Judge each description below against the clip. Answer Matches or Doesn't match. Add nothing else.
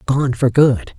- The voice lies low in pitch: Matches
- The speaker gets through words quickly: Doesn't match